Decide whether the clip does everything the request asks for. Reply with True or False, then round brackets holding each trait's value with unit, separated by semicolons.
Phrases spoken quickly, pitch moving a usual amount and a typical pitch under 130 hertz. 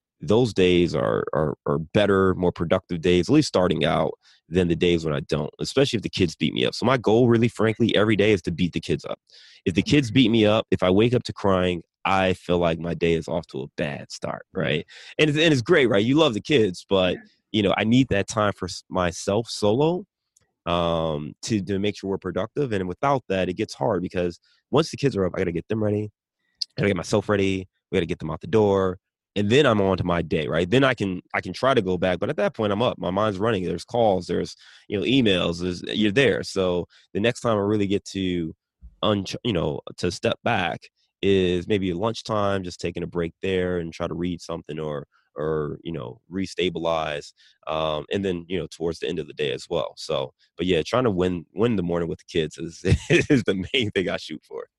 True (245 wpm; 3.6 semitones; 95 Hz)